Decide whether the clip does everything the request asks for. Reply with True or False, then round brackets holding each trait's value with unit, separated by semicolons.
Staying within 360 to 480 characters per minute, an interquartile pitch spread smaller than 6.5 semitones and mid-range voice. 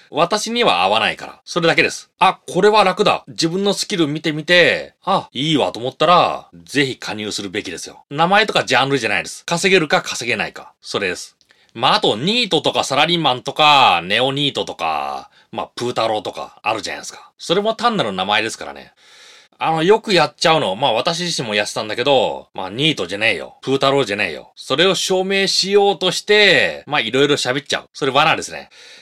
True (420 characters per minute; 6.1 semitones; 170 Hz)